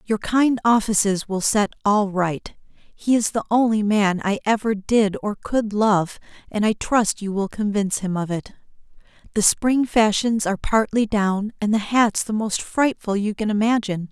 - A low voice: No, high, 210 Hz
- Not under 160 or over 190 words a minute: Yes, average, 180 wpm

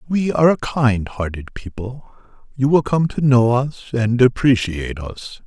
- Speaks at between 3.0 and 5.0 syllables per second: Yes, 4.3 syllables/s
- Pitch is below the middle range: Yes, low, 125 Hz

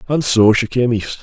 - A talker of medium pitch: No, low, 115 Hz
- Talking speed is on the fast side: Yes, fast, 245 wpm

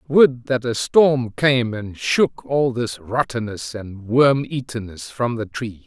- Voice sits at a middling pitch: No, low, 120 Hz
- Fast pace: No, average, 165 wpm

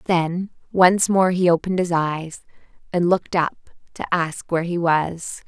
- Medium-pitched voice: Yes, medium, 175 Hz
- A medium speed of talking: Yes, average, 165 wpm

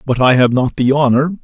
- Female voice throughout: No, male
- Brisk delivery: Yes, fast, 250 wpm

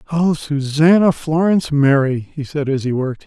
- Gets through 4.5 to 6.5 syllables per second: Yes, 5.0 syllables/s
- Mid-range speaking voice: Yes, medium, 150 Hz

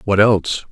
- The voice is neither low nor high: No, low, 105 Hz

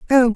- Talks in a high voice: Yes, high, 245 Hz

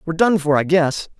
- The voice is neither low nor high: Yes, medium, 165 Hz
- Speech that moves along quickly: Yes, fast, 250 wpm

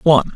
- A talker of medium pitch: Yes, medium, 145 Hz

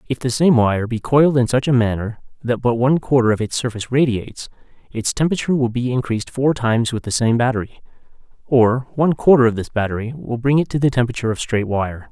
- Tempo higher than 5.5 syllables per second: Yes, 6.5 syllables/s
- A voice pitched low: Yes, low, 120 Hz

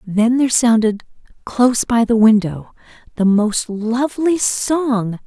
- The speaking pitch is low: No, high, 235 Hz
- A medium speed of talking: No, slow, 125 wpm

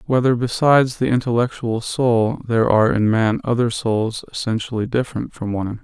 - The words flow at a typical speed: Yes, average, 165 wpm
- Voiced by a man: Yes, male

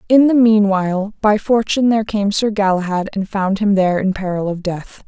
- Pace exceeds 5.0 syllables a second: Yes, 5.5 syllables/s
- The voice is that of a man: No, female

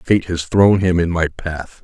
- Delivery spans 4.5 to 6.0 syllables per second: No, 3.9 syllables/s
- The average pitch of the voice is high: No, very low, 85 Hz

